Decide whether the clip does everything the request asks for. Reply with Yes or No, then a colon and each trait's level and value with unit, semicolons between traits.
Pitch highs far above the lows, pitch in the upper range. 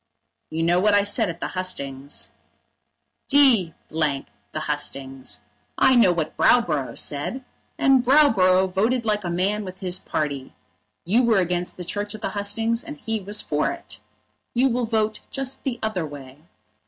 Yes: wide, 5.8 semitones; high, 195 Hz